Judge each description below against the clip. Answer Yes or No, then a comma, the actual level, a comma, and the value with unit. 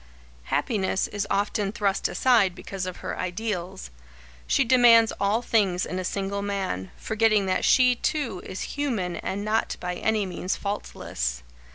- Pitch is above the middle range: Yes, high, 200 Hz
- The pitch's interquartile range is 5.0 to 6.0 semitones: No, average, 3.2 semitones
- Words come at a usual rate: Yes, average, 150 wpm